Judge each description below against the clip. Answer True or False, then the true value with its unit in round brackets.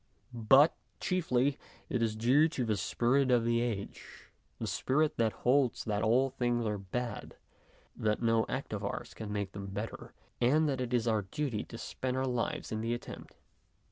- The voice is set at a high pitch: False (120 Hz)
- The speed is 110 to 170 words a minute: False (180 wpm)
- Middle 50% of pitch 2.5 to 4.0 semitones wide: True (3.2 semitones)